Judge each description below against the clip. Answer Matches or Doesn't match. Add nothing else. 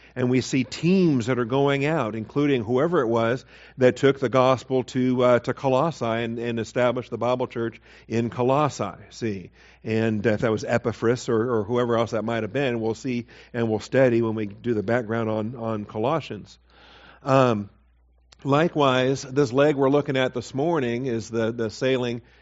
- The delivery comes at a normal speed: Matches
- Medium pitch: Doesn't match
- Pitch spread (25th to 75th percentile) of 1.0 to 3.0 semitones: Matches